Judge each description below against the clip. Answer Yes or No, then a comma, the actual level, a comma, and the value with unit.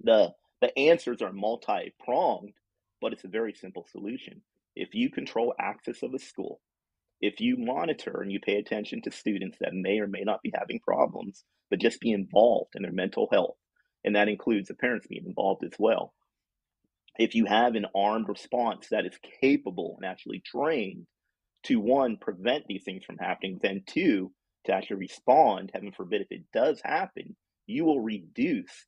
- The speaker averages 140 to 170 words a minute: No, average, 180 wpm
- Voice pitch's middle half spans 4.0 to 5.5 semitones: Yes, average, 5.1 semitones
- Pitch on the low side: Yes, low, 110 Hz